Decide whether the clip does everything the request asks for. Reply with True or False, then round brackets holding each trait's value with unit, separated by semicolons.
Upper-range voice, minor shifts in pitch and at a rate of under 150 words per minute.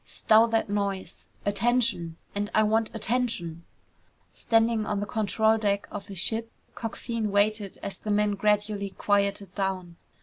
True (205 Hz; 1.8 semitones; 140 wpm)